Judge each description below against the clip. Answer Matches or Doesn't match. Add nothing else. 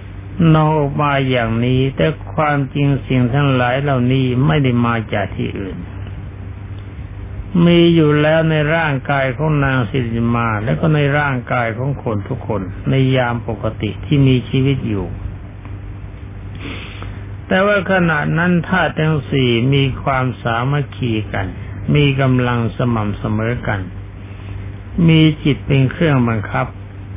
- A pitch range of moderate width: Doesn't match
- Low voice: Matches